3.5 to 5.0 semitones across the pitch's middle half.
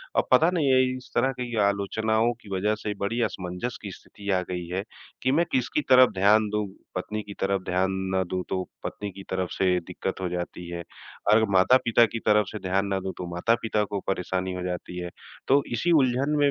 Yes: average, 4.2 semitones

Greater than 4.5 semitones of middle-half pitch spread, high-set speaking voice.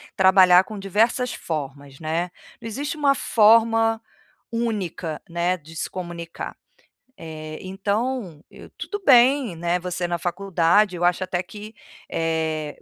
No: average, 5.0 semitones; medium, 180 Hz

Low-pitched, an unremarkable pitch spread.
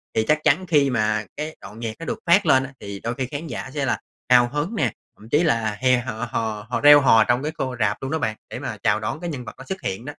Yes: low, 130 Hz; average, 4.8 semitones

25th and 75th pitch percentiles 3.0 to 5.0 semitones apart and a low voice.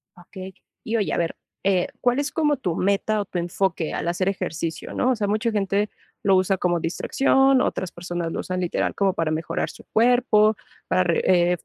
No: average, 3.7 semitones; high, 190 Hz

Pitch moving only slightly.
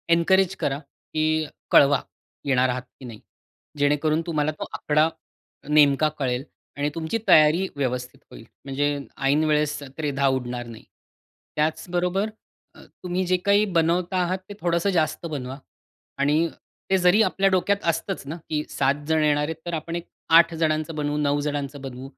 No: average, 3.2 semitones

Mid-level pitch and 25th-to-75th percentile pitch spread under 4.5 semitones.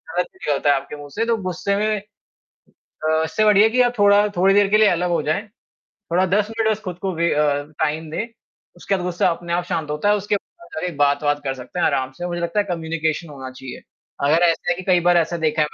No: medium, 175 Hz; average, 4.8 semitones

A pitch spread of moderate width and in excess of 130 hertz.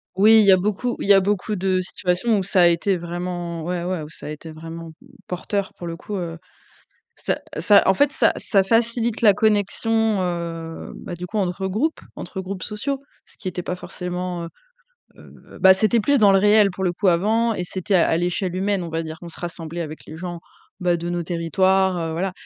Yes: average, 3.1 semitones; medium, 185 Hz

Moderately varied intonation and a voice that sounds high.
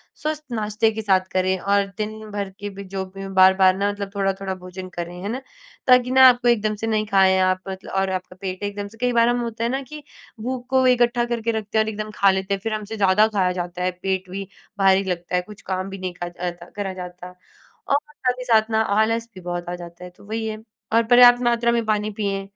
Yes: average, 3.3 semitones; high, 205 Hz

